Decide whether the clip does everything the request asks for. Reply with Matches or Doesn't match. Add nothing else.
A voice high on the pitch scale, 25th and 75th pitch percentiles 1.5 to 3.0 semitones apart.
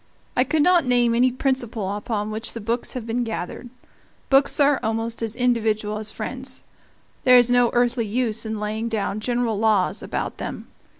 Matches